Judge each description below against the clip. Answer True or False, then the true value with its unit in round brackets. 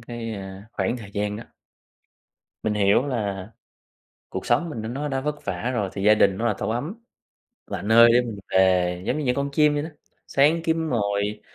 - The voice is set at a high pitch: False (115 Hz)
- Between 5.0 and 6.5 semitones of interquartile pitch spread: True (5.4 semitones)